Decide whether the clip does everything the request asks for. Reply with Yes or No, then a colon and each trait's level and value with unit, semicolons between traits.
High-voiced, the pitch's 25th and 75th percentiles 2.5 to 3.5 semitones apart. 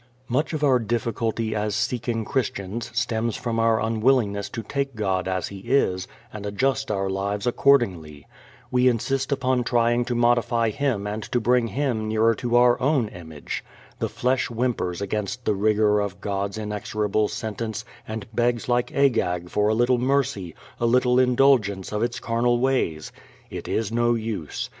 No: low, 115 Hz; average, 3.1 semitones